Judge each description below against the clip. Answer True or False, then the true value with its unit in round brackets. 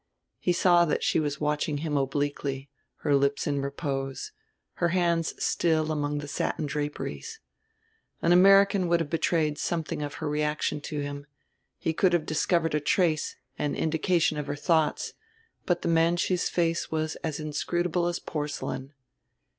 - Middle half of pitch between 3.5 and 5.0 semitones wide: False (2.7 semitones)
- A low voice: False (155 Hz)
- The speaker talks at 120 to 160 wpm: True (155 wpm)